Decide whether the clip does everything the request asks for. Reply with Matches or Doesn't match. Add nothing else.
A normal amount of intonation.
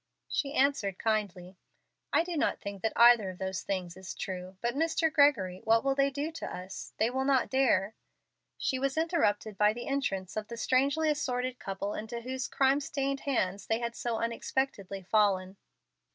Doesn't match